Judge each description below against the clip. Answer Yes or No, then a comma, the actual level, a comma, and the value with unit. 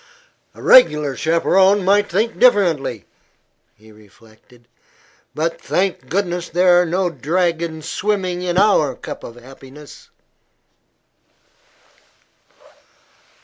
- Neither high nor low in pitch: Yes, medium, 170 Hz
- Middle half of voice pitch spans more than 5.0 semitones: Yes, wide, 5.5 semitones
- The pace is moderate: No, slow, 95 wpm